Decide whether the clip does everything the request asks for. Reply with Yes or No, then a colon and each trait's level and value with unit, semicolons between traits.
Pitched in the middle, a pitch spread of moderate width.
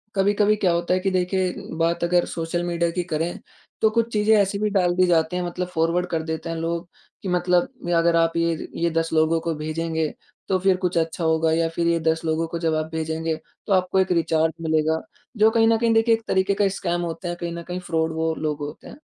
No: medium, 170 Hz; narrow, 2.2 semitones